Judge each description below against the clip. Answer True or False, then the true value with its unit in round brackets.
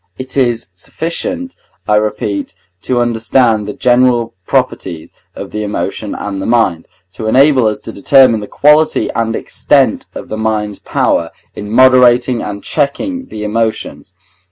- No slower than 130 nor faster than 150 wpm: True (145 wpm)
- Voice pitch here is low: True (115 Hz)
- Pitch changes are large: False (3.6 semitones)